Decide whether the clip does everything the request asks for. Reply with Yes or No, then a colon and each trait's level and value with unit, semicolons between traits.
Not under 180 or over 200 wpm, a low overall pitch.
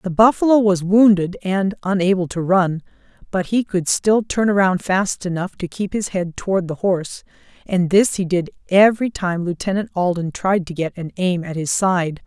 No: average, 190 wpm; medium, 185 Hz